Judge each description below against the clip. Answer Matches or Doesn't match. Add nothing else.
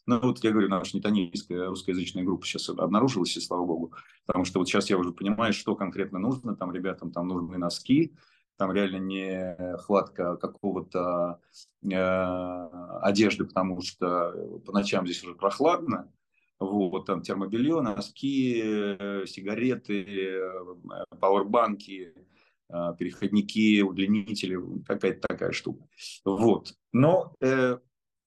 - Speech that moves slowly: Doesn't match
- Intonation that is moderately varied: Doesn't match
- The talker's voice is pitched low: Matches